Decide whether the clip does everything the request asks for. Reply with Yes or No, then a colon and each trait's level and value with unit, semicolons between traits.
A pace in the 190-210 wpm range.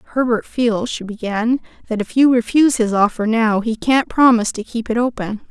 Yes: average, 195 wpm